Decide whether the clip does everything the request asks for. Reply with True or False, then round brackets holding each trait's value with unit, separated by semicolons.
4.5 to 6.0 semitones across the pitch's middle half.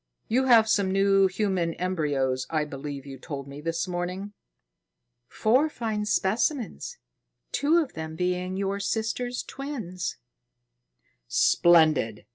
True (5.6 semitones)